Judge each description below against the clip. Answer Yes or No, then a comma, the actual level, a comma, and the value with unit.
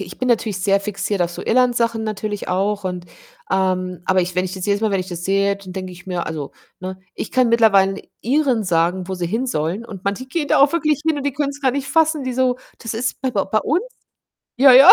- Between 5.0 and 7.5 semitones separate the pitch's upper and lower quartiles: Yes, wide, 5.5 semitones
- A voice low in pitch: No, high, 205 Hz